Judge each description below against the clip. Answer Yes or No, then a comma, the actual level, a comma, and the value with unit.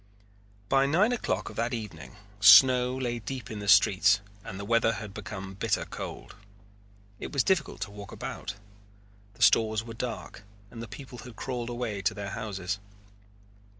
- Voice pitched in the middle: No, low, 110 Hz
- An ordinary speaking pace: Yes, average, 165 wpm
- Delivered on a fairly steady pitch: No, average, 3.6 semitones